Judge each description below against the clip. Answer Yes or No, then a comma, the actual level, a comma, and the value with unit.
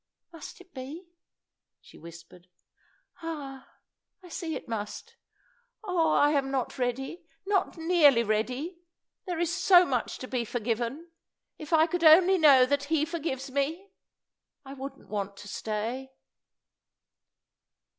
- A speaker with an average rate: No, slow, 125 wpm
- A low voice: No, very high, 285 Hz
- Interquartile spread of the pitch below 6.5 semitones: Yes, average, 5.1 semitones